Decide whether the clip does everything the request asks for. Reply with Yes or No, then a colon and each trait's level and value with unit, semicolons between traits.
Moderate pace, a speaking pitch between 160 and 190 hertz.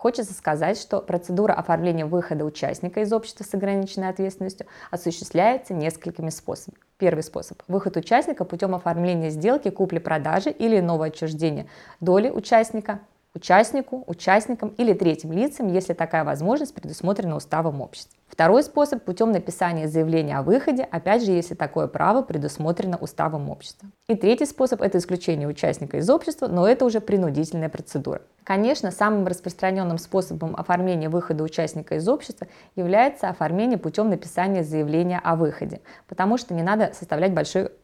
Yes: average, 140 wpm; medium, 185 Hz